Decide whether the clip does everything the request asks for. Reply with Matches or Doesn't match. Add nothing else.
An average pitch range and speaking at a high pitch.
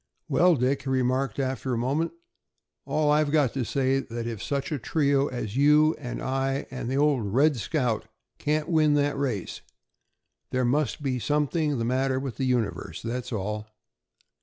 Doesn't match